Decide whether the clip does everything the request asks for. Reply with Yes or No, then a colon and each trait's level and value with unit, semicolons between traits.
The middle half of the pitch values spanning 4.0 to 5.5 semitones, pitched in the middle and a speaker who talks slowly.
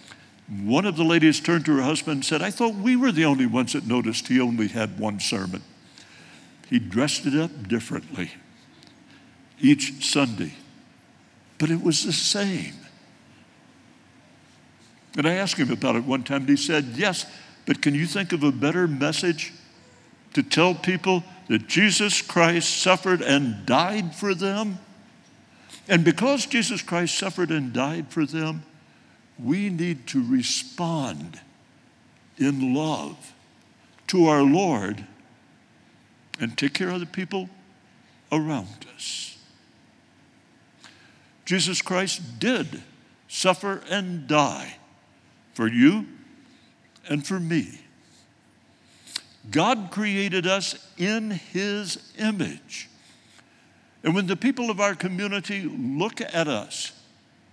Yes: average, 5.0 semitones; medium, 175 Hz; slow, 125 wpm